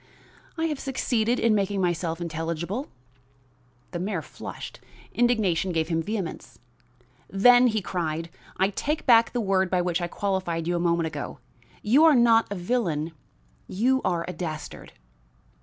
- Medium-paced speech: Yes, average, 150 wpm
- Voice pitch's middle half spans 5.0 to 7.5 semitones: Yes, wide, 5.4 semitones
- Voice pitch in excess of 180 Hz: Yes, high, 190 Hz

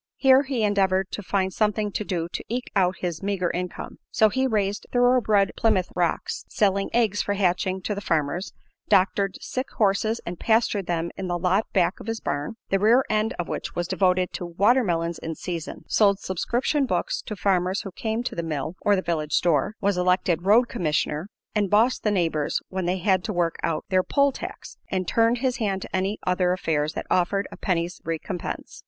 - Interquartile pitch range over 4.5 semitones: No, average, 3.4 semitones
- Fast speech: No, average, 195 wpm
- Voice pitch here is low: No, high, 195 Hz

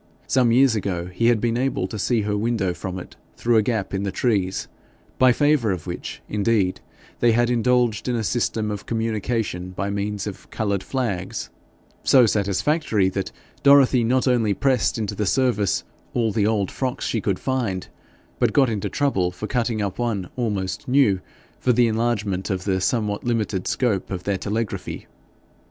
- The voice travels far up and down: No, average, 3.6 semitones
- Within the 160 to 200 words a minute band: Yes, average, 175 wpm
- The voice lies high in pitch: No, low, 110 Hz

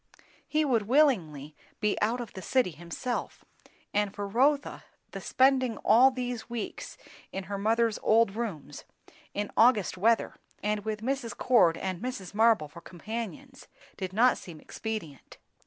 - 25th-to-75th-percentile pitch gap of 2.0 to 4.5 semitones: Yes, average, 4.2 semitones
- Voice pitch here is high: Yes, high, 220 Hz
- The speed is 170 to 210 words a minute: No, average, 145 wpm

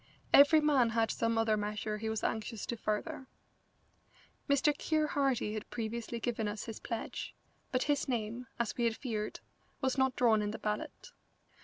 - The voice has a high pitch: Yes, high, 230 Hz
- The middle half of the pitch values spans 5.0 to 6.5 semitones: No, average, 3.4 semitones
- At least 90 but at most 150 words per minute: No, average, 170 wpm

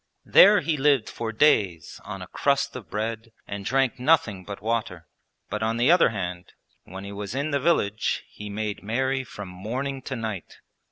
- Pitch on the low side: Yes, low, 110 Hz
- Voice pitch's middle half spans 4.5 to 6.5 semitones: Yes, average, 4.9 semitones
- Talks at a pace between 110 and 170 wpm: No, average, 180 wpm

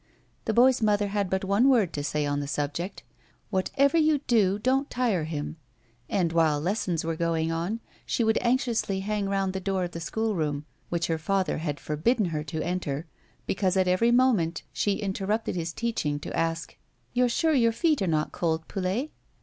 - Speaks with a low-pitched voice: No, high, 190 Hz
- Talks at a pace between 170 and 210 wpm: Yes, average, 195 wpm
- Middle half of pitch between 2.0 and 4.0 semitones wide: No, wide, 5.5 semitones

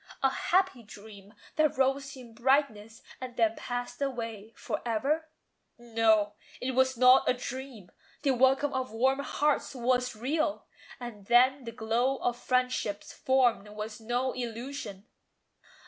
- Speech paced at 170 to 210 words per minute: No, average, 140 wpm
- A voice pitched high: Yes, very high, 250 Hz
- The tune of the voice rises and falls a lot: No, average, 3.0 semitones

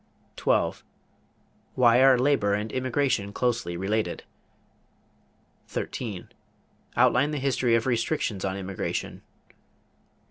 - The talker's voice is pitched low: Yes, low, 120 Hz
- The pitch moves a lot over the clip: No, average, 4.3 semitones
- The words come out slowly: Yes, slow, 95 wpm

